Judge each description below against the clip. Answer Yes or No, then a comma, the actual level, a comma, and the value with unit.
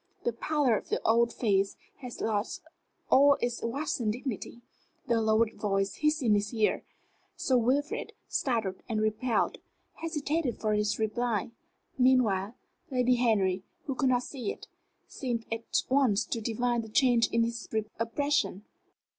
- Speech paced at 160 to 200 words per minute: No, average, 145 wpm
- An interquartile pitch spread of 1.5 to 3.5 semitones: Yes, average, 3.0 semitones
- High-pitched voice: Yes, high, 230 Hz